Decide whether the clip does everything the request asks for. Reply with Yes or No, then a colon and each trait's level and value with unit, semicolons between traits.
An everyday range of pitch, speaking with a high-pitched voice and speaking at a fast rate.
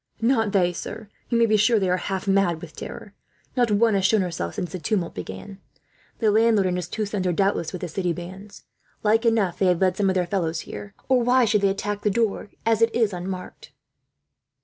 Yes: average, 3.5 semitones; high, 195 Hz; fast, 225 wpm